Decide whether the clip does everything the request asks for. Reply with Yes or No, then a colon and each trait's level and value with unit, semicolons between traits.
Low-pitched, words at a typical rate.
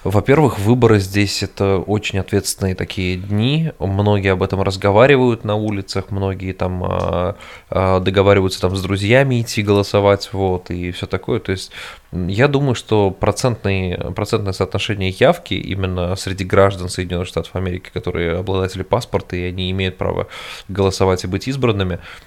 Yes: very low, 95 Hz; average, 135 wpm